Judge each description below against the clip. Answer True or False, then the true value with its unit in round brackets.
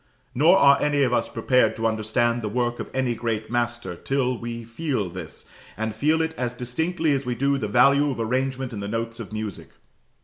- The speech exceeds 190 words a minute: True (205 wpm)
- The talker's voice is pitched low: True (120 Hz)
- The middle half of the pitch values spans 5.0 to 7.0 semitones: False (3.5 semitones)